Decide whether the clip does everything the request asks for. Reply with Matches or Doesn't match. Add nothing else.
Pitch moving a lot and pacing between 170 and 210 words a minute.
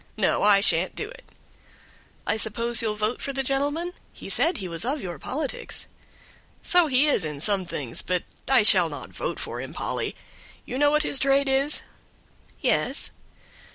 Matches